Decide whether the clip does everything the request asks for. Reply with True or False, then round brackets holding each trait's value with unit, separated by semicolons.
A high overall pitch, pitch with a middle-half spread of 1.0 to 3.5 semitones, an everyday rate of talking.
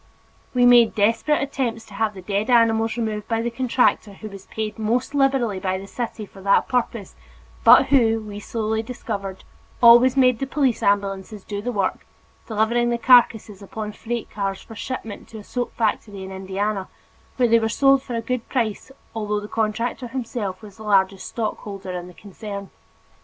True (220 Hz; 2.9 semitones; 180 wpm)